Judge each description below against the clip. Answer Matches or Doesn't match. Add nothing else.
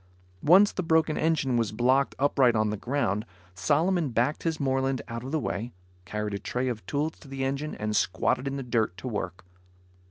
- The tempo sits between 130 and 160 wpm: Doesn't match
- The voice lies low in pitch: Matches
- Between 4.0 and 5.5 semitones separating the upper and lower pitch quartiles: Matches